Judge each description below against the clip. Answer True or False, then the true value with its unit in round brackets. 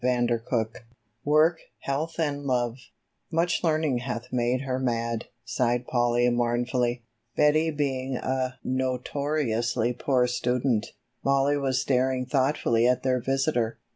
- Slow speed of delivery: True (120 wpm)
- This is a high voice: False (130 Hz)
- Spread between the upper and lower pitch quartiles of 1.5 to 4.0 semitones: True (2.4 semitones)